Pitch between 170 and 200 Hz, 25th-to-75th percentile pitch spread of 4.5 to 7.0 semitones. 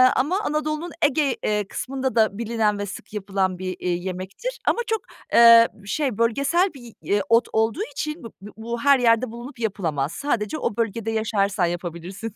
No: high, 225 Hz; average, 5.2 semitones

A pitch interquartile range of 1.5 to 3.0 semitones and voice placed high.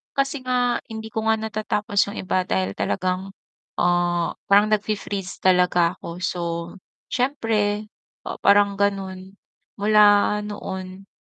Yes: narrow, 2.6 semitones; high, 200 Hz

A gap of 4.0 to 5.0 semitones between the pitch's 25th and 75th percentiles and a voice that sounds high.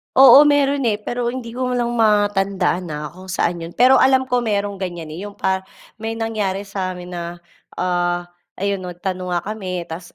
Yes: average, 4.5 semitones; high, 195 Hz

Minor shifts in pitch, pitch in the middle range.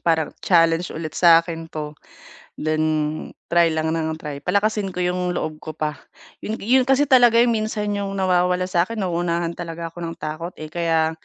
No: average, 3.5 semitones; medium, 170 Hz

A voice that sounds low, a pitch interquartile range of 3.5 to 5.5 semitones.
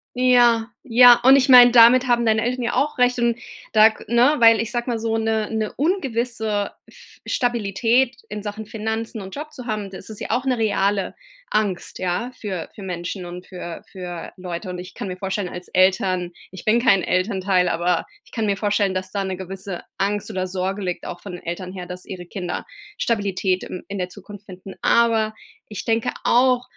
No: high, 210 Hz; average, 4.0 semitones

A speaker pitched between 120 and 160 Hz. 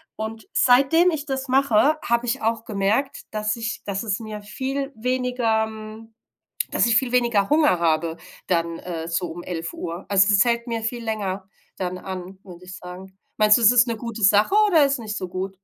No: high, 220 Hz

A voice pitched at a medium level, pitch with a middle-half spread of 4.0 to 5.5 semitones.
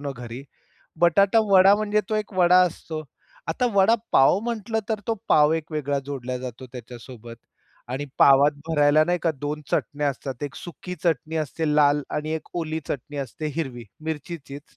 Yes: medium, 150 Hz; average, 4.3 semitones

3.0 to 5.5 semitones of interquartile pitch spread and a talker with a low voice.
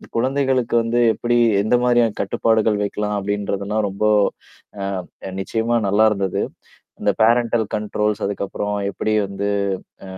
No: narrow, 2.5 semitones; low, 105 Hz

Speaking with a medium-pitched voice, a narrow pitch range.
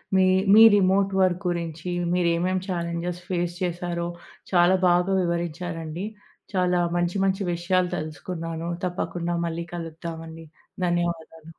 Yes: medium, 175 Hz; narrow, 1.3 semitones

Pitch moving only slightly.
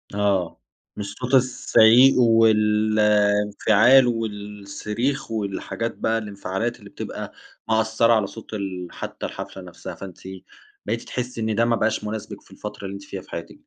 Yes: narrow, 2.0 semitones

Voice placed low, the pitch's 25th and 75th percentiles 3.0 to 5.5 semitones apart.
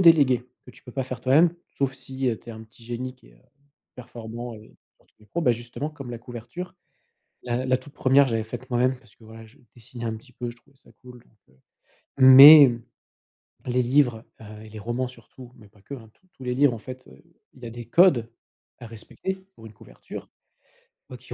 No: low, 125 Hz; narrow, 2.5 semitones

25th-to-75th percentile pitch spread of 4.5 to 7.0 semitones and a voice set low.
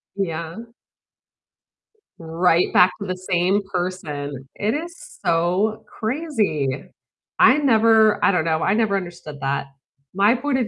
No: average, 4.9 semitones; medium, 185 Hz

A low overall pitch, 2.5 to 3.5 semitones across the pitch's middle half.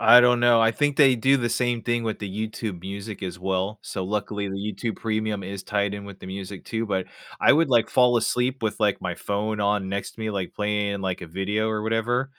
Yes: low, 105 Hz; average, 2.9 semitones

